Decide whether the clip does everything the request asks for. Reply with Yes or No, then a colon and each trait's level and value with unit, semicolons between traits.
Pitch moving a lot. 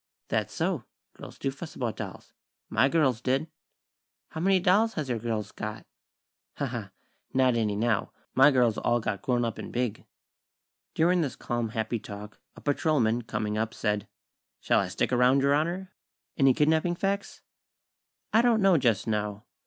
Yes: wide, 6.2 semitones